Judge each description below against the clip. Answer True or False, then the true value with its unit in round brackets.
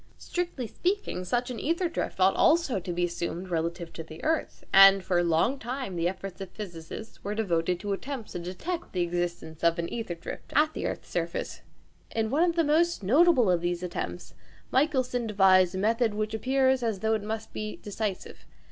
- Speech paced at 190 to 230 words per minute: True (195 wpm)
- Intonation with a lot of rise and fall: True (6.6 semitones)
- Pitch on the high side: True (205 Hz)